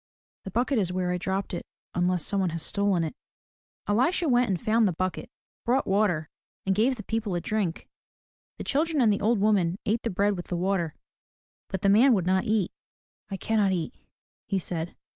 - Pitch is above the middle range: Yes, high, 195 Hz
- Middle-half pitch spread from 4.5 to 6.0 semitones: No, average, 3.6 semitones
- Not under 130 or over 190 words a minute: No, average, 200 wpm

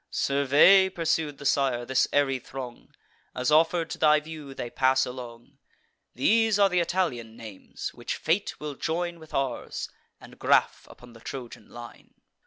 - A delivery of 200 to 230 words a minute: No, average, 155 wpm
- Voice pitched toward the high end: No, medium, 140 Hz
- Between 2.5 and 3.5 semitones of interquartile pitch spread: No, average, 4.6 semitones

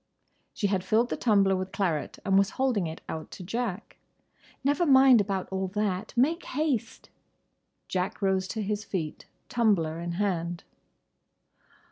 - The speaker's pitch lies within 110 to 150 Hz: No, high, 200 Hz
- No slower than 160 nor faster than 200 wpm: No, average, 145 wpm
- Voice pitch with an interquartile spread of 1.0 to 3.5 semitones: No, average, 4.0 semitones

